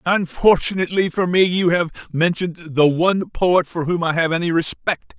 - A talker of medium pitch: Yes, medium, 170 Hz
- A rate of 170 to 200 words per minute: Yes, average, 175 wpm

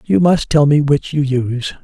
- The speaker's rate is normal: No, fast, 230 wpm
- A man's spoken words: Yes, male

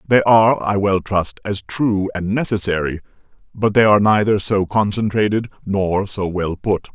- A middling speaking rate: Yes, average, 165 wpm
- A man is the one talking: Yes, male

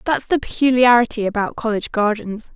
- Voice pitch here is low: No, high, 230 Hz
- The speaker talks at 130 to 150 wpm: Yes, average, 140 wpm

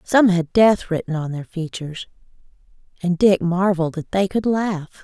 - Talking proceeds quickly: No, average, 165 wpm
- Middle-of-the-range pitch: Yes, medium, 180 Hz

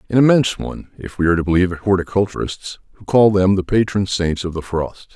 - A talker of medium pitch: No, very low, 95 Hz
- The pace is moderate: No, fast, 210 wpm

